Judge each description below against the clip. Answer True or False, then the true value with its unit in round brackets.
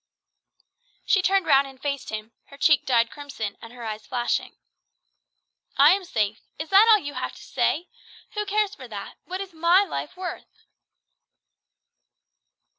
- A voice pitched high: True (290 Hz)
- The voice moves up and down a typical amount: False (8.2 semitones)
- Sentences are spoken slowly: False (155 wpm)